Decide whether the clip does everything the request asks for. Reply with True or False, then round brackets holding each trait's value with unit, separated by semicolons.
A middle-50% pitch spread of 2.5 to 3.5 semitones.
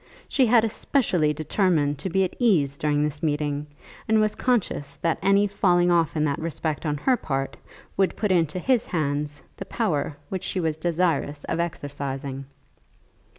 False (4.7 semitones)